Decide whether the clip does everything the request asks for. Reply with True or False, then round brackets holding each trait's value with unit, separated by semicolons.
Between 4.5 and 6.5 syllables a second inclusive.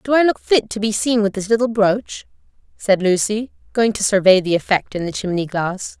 True (5.2 syllables/s)